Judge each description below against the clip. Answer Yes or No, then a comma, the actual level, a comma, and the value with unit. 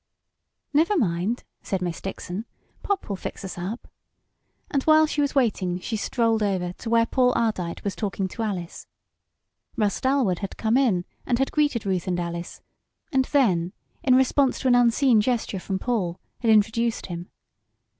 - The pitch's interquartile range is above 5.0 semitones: Yes, wide, 5.4 semitones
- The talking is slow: No, average, 165 wpm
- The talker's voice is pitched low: No, high, 220 Hz